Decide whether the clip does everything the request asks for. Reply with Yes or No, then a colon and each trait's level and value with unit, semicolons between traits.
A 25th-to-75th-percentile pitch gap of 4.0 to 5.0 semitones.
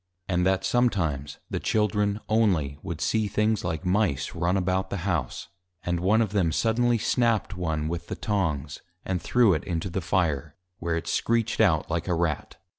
Yes: average, 4.3 semitones